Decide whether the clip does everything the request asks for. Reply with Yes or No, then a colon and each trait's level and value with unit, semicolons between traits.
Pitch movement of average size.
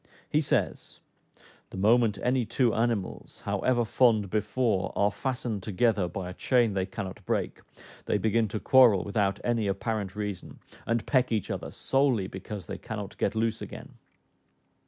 Yes: average, 3.2 semitones